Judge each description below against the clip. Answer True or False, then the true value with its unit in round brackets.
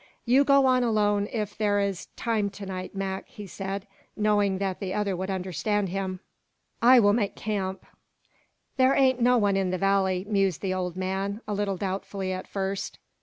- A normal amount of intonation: False (1.8 semitones)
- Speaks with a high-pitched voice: True (200 Hz)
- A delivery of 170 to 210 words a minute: True (180 wpm)